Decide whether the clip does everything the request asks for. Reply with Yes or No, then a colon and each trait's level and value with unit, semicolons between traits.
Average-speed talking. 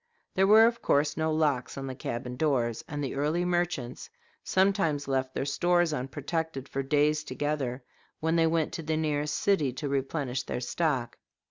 Yes: average, 170 wpm